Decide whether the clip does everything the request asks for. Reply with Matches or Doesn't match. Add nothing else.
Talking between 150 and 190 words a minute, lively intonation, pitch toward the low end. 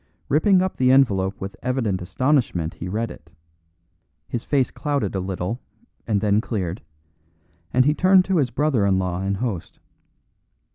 Matches